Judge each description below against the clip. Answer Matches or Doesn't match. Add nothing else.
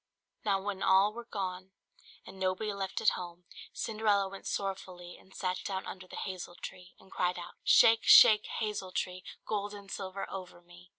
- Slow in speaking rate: Doesn't match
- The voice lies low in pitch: Doesn't match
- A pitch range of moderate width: Doesn't match